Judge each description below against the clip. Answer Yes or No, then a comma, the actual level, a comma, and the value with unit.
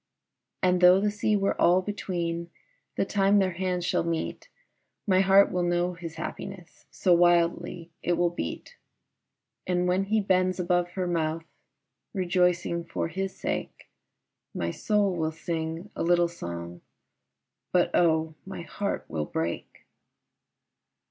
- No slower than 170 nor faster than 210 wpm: No, slow, 135 wpm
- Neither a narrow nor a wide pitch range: No, narrow, 2.0 semitones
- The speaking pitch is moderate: Yes, medium, 175 Hz